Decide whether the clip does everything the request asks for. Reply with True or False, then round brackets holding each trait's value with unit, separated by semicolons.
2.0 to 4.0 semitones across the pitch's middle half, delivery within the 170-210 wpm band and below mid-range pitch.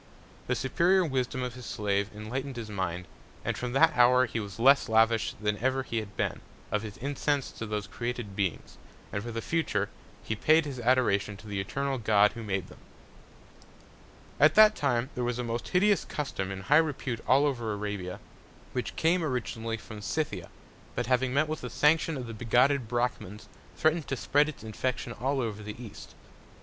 False (4.5 semitones; 185 wpm; 120 Hz)